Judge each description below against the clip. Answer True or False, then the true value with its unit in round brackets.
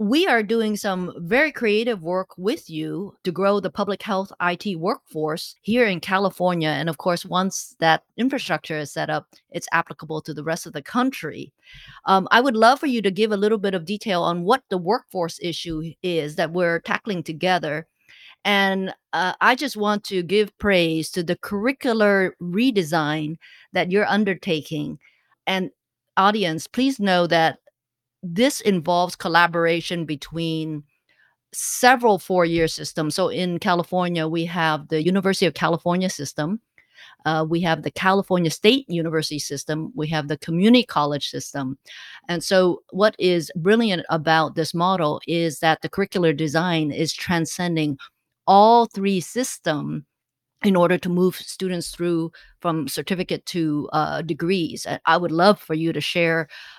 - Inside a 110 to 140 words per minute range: False (155 wpm)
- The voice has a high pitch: False (175 Hz)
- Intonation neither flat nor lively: True (3.6 semitones)